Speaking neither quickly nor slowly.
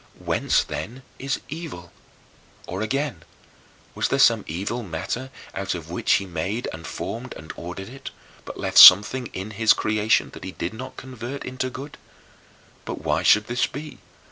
Yes: average, 165 wpm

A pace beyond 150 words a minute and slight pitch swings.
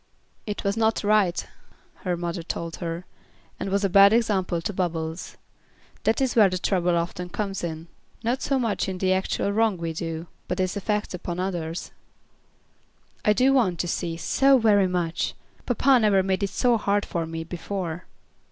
No: average, 175 wpm; average, 3.5 semitones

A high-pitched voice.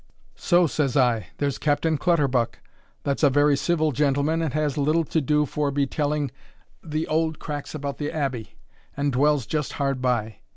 No: medium, 145 Hz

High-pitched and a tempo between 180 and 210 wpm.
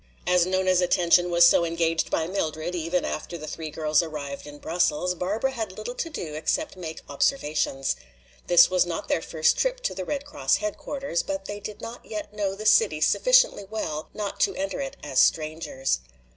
No: medium, 180 Hz; average, 185 wpm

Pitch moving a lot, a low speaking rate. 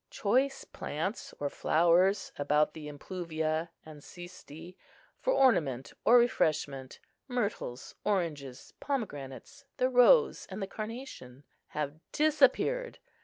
Yes: wide, 8.6 semitones; slow, 105 wpm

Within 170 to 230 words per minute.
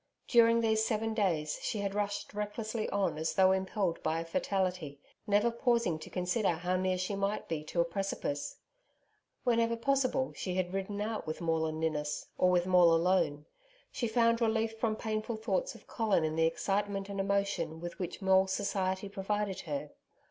Yes: average, 175 wpm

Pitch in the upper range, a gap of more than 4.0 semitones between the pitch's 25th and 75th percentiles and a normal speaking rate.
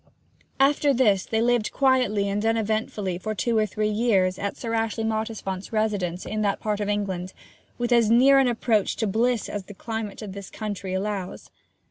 No: high, 215 Hz; narrow, 2.4 semitones; average, 180 wpm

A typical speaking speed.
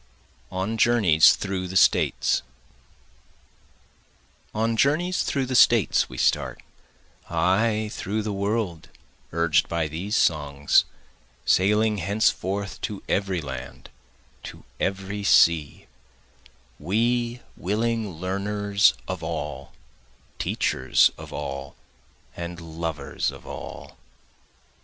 No: slow, 95 wpm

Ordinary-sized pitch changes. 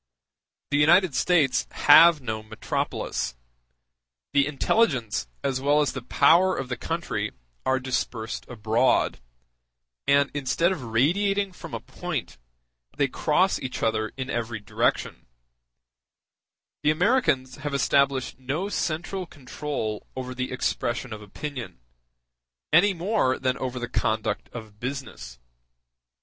Yes: average, 4.4 semitones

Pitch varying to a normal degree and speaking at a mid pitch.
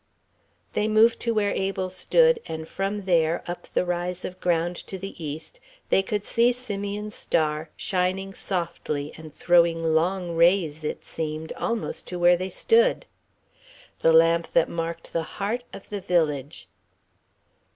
Yes: average, 3.4 semitones; medium, 180 Hz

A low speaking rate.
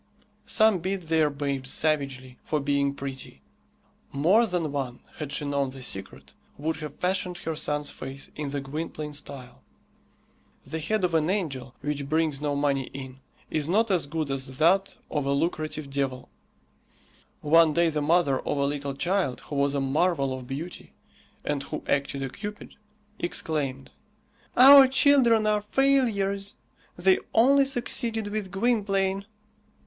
No: average, 150 wpm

